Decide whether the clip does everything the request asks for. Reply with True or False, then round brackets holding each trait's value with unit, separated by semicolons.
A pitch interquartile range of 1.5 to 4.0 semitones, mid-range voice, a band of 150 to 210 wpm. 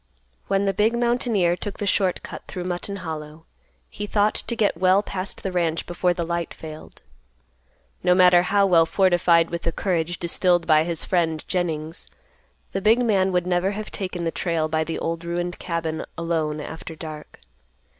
True (2.7 semitones; 175 Hz; 175 wpm)